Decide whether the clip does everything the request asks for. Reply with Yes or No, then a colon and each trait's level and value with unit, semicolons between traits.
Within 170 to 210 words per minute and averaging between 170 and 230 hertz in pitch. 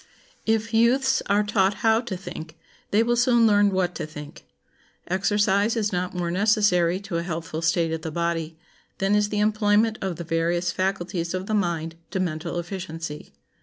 Yes: average, 175 wpm; medium, 185 Hz